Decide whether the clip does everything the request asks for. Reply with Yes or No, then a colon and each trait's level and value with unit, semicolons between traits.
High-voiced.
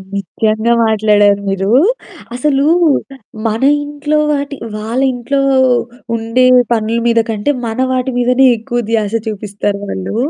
Yes: high, 225 Hz